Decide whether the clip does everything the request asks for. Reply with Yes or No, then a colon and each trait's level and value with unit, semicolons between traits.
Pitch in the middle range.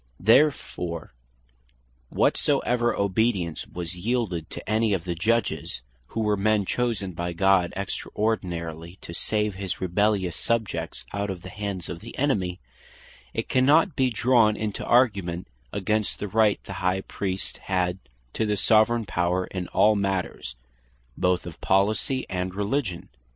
No: low, 100 Hz